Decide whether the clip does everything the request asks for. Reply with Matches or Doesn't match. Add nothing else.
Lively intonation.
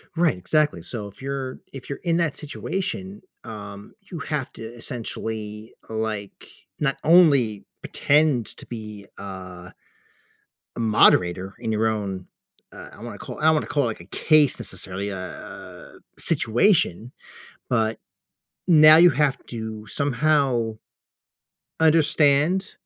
Matches